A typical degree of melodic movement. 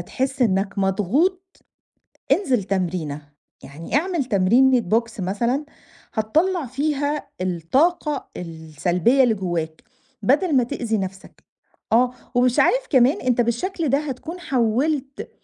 No: wide, 7.0 semitones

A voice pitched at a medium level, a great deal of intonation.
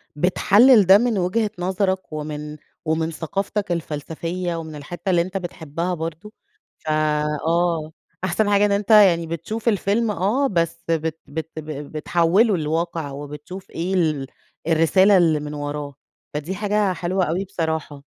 No: medium, 170 Hz; average, 3.8 semitones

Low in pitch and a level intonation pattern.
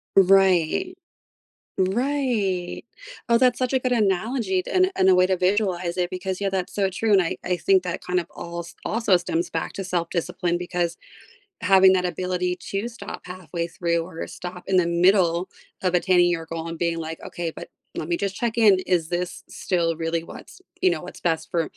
No: medium, 180 Hz; narrow, 2.2 semitones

